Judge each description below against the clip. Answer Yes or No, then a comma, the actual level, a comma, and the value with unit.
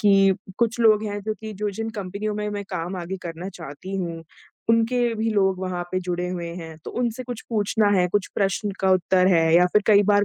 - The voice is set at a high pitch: Yes, high, 195 Hz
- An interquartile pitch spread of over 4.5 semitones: No, average, 2.9 semitones